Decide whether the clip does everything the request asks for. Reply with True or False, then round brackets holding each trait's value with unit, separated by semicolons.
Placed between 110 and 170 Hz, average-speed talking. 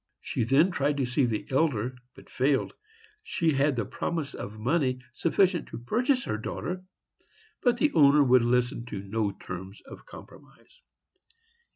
True (135 Hz; 155 wpm)